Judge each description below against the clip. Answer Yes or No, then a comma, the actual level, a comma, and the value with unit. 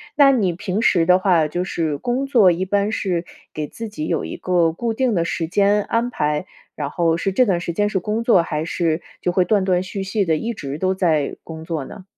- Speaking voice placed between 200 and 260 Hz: No, medium, 185 Hz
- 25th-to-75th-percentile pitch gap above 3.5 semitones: Yes, average, 4.0 semitones